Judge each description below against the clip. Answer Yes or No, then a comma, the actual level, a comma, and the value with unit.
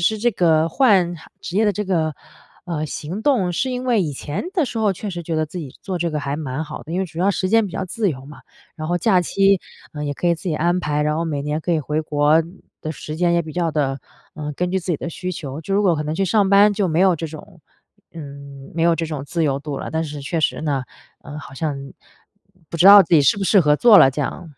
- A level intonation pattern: No, average, 3.9 semitones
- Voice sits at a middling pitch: Yes, medium, 165 Hz